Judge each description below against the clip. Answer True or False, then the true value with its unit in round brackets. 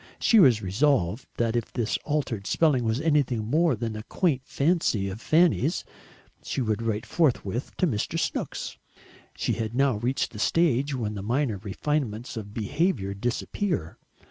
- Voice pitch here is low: True (120 Hz)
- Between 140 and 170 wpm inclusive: True (155 wpm)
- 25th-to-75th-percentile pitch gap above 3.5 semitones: True (5.5 semitones)